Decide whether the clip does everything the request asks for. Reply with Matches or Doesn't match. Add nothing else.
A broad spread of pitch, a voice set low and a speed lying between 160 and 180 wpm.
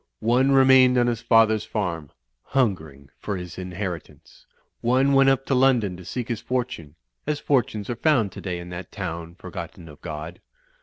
Matches